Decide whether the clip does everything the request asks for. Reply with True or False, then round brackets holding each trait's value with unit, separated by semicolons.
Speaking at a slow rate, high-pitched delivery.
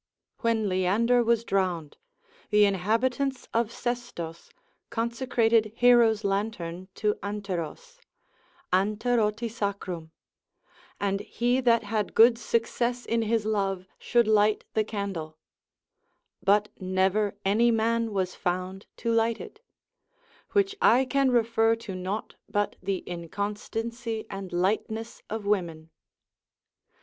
True (110 wpm; 215 Hz)